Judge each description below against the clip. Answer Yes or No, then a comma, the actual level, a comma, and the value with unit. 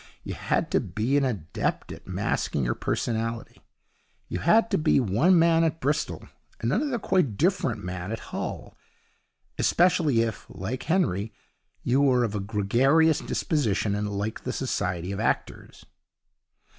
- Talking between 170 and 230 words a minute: No, average, 145 wpm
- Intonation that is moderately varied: No, wide, 7.8 semitones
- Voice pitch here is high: No, low, 120 Hz